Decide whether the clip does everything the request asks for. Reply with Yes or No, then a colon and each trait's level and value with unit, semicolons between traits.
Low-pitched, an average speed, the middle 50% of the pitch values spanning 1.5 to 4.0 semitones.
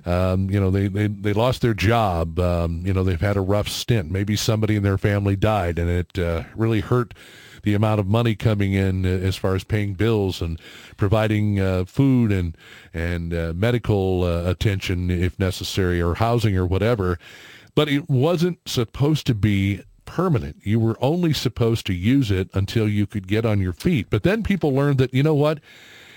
Yes: low, 105 Hz; average, 195 wpm; average, 3.6 semitones